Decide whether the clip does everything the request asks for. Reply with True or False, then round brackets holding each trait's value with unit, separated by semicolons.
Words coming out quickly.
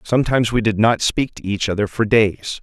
True (230 wpm)